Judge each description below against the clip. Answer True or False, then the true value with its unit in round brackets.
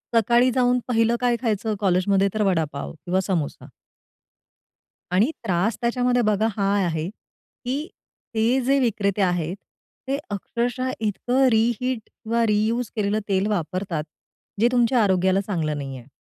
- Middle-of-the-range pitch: False (215 Hz)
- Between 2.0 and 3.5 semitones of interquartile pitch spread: False (4.3 semitones)